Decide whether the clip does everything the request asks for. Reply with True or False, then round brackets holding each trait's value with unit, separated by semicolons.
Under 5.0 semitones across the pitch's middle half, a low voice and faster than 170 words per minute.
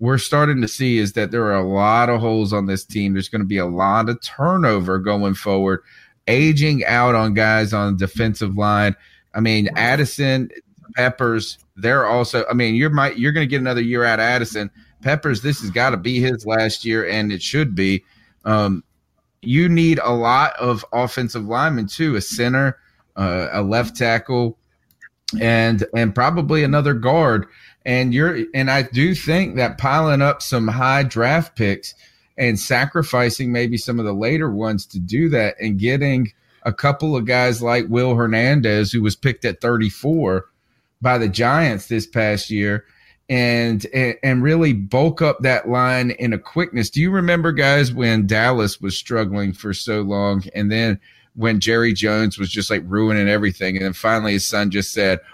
True (4.0 semitones; 115 Hz; 180 wpm)